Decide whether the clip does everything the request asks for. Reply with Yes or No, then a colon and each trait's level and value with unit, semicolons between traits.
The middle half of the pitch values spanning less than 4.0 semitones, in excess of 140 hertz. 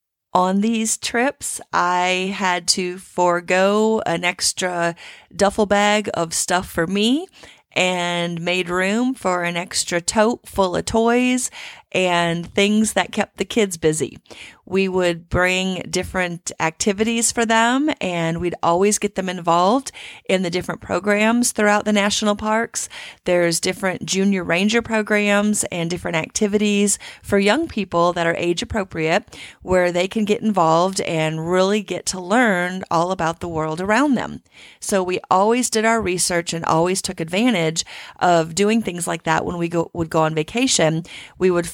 Yes: average, 3.5 semitones; medium, 185 Hz